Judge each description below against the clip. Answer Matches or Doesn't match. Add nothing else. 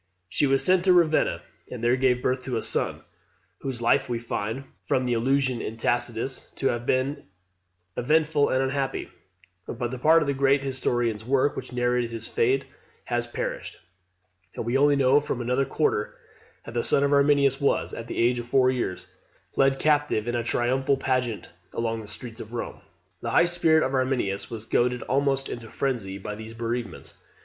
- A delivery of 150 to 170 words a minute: Doesn't match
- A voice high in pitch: Doesn't match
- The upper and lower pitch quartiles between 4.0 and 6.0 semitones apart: Doesn't match